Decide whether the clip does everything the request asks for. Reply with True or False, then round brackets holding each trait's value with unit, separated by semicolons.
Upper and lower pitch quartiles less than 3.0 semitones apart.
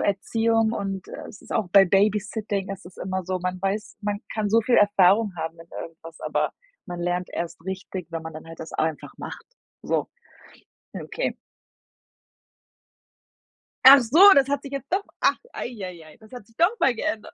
False (4.2 semitones)